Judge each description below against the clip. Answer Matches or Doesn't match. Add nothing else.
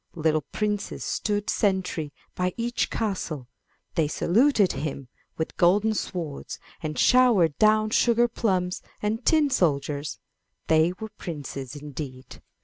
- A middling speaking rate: Doesn't match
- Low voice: Doesn't match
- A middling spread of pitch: Doesn't match